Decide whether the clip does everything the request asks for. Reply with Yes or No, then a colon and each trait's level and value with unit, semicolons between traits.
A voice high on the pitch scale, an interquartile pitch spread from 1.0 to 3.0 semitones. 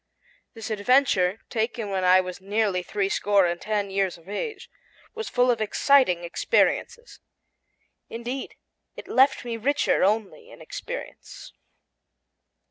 No: high, 215 Hz; average, 4.9 semitones